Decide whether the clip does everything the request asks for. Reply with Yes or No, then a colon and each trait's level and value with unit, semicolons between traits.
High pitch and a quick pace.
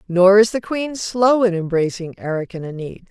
No: high, 195 Hz; average, 195 wpm